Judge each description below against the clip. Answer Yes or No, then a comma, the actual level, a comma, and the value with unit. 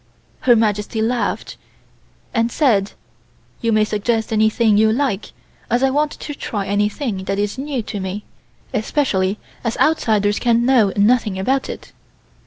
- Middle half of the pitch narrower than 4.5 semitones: Yes, average, 3.3 semitones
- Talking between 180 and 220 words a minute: No, average, 145 wpm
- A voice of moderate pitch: No, high, 220 Hz